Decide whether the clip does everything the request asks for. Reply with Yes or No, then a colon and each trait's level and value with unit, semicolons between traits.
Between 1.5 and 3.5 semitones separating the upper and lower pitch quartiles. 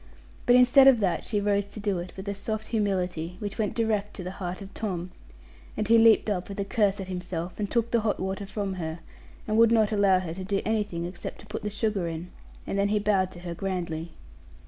Yes: average, 2.8 semitones